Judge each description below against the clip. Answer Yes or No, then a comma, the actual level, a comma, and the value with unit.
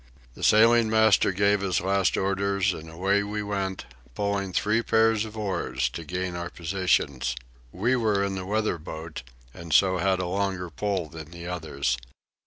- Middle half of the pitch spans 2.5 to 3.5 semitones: Yes, average, 3.0 semitones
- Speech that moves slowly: No, average, 170 wpm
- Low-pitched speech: Yes, very low, 95 Hz